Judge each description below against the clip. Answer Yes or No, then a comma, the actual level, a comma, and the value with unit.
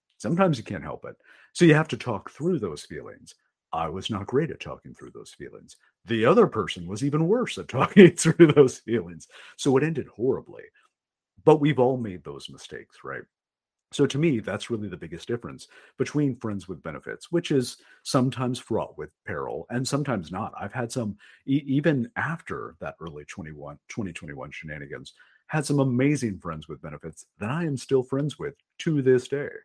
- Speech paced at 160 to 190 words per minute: Yes, average, 180 wpm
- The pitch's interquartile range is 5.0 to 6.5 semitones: Yes, wide, 5.4 semitones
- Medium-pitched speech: No, low, 130 Hz